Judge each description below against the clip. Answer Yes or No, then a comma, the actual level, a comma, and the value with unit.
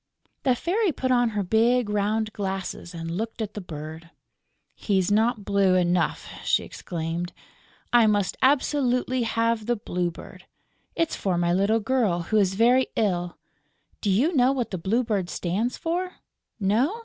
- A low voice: No, high, 210 Hz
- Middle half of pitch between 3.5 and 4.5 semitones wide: No, average, 4.9 semitones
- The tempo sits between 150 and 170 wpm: Yes, average, 160 wpm